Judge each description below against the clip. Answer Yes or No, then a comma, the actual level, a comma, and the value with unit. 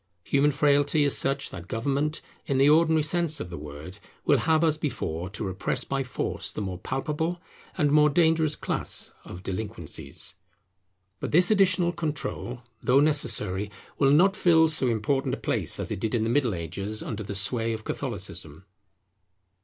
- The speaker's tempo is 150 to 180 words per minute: Yes, average, 170 wpm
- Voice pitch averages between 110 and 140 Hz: Yes, low, 135 Hz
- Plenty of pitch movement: Yes, wide, 7.0 semitones